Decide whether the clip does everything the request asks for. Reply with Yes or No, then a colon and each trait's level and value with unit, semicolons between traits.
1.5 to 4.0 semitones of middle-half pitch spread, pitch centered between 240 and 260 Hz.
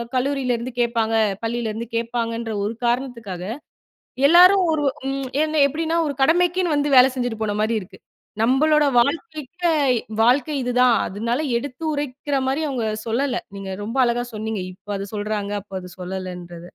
No: average, 4.5 semitones; high, 245 Hz